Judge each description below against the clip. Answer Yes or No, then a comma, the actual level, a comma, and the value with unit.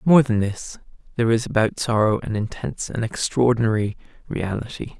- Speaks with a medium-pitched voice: No, low, 115 Hz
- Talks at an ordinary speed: Yes, average, 145 wpm